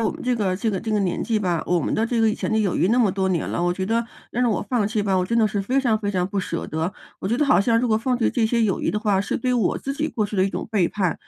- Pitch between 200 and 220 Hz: Yes, high, 215 Hz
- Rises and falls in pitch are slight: No, average, 3.5 semitones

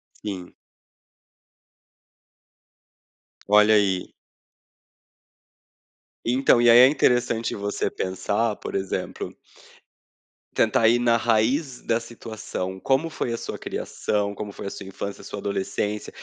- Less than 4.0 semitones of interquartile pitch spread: Yes, average, 2.8 semitones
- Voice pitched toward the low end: Yes, low, 110 Hz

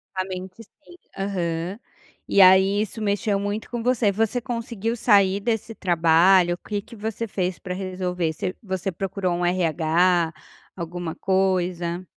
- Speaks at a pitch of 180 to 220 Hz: Yes, high, 190 Hz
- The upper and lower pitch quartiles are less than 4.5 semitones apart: Yes, narrow, 2.6 semitones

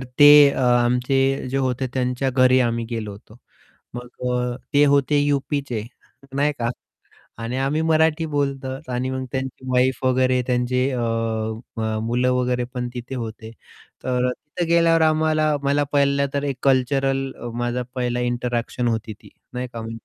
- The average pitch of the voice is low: Yes, low, 130 Hz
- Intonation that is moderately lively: No, narrow, 2.3 semitones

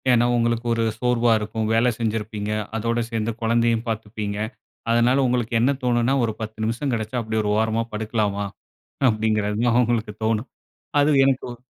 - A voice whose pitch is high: No, low, 115 Hz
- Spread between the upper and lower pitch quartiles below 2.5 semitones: Yes, narrow, 1.6 semitones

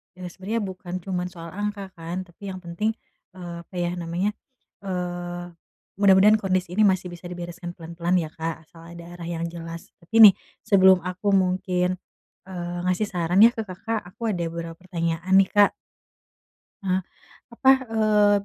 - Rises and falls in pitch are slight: Yes, narrow, 2.3 semitones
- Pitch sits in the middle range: Yes, medium, 180 Hz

